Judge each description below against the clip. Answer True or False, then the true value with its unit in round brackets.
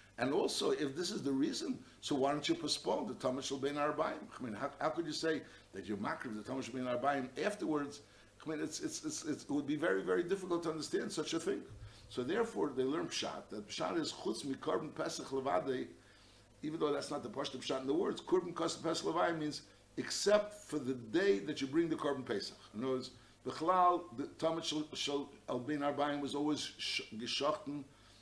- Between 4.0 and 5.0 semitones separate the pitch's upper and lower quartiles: True (4.5 semitones)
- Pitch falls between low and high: True (150 Hz)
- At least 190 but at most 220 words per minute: True (205 wpm)